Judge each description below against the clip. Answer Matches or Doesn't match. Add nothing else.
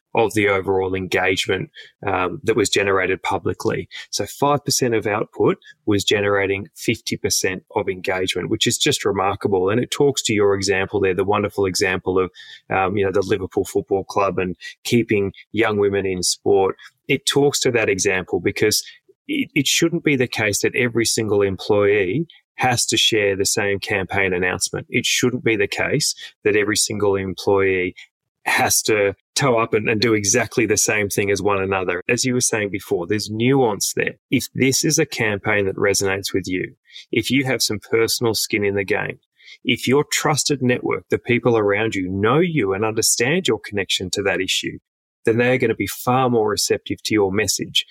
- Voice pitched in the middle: Doesn't match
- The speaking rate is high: Doesn't match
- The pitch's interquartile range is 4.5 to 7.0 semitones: Matches